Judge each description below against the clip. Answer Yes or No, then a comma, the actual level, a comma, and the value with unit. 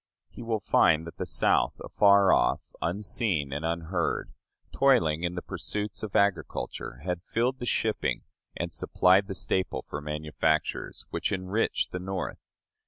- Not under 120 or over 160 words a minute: Yes, average, 145 wpm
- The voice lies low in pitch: Yes, very low, 95 Hz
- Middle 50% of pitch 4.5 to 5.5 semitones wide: No, average, 4.1 semitones